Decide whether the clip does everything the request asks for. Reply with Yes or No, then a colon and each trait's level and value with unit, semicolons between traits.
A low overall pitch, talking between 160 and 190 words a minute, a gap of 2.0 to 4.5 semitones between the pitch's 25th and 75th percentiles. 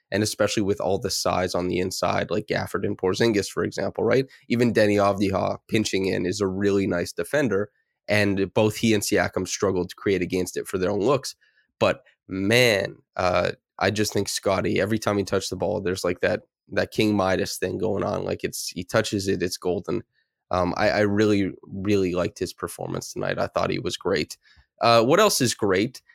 No: low, 100 Hz; average, 200 wpm; narrow, 2.4 semitones